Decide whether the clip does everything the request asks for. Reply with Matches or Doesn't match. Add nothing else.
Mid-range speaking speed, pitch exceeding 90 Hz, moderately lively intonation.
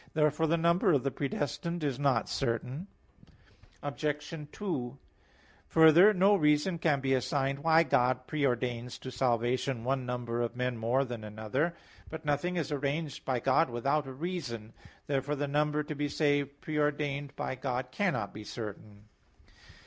Matches